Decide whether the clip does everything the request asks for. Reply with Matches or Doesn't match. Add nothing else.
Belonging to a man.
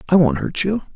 Matches